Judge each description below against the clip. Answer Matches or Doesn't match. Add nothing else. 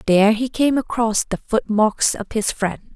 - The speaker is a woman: Matches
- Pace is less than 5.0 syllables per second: Matches